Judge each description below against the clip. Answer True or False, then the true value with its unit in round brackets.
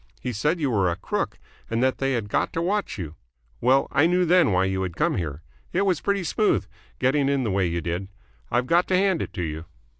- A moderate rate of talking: False (240 wpm)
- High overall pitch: False (125 Hz)